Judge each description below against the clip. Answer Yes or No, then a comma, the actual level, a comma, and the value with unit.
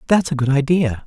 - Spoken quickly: Yes, fast, 225 wpm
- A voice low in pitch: No, medium, 145 Hz